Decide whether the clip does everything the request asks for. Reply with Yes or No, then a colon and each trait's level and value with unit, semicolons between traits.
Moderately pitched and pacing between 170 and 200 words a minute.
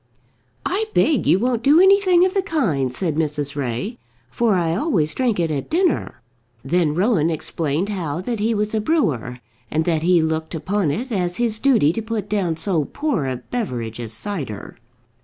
Yes: medium, 180 Hz; average, 180 wpm